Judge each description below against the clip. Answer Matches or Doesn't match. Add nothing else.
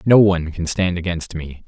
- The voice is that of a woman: Doesn't match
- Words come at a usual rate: Doesn't match